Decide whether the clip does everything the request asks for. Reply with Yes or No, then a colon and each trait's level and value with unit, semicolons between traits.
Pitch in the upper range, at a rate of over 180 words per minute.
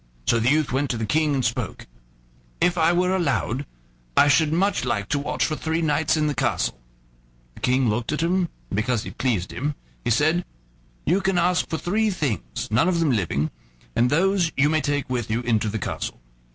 No: medium, 145 Hz; fast, 205 wpm